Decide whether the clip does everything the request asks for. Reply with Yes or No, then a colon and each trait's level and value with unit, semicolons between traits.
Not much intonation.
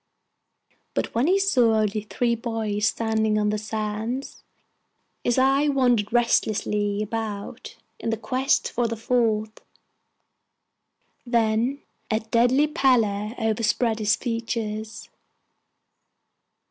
Yes: narrow, 2.3 semitones